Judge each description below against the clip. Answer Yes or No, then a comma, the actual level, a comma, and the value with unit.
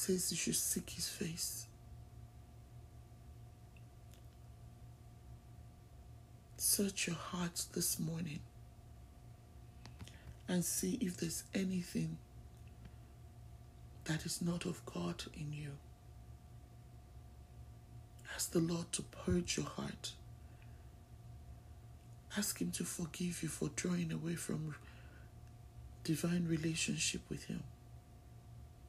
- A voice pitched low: No, medium, 145 Hz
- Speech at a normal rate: No, slow, 90 wpm